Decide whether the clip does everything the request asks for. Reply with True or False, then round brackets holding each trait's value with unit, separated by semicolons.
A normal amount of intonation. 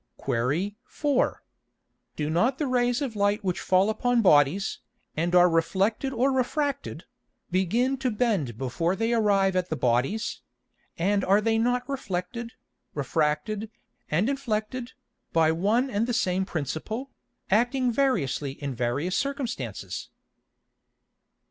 False (6.8 semitones)